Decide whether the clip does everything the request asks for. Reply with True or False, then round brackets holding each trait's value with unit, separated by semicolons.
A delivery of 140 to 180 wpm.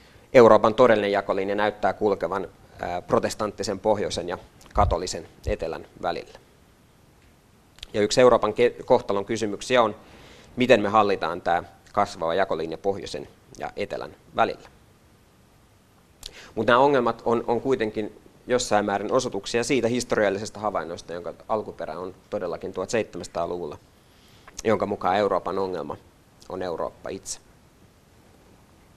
False (105 wpm)